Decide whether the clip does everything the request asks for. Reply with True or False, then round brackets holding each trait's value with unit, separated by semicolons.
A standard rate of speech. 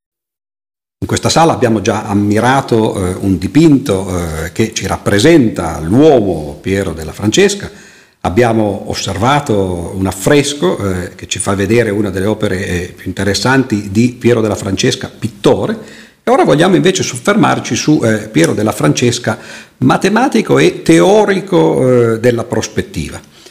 True (135 wpm)